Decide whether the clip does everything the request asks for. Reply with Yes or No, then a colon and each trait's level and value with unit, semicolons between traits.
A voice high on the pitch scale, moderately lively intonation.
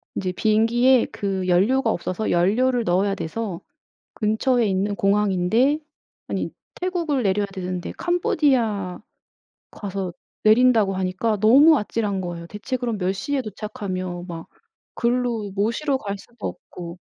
Yes: high, 210 Hz; average, 4.6 semitones